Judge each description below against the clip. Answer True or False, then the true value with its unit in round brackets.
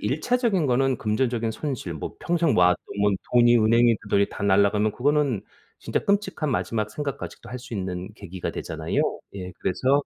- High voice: False (120 Hz)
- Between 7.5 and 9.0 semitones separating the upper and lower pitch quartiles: False (5.6 semitones)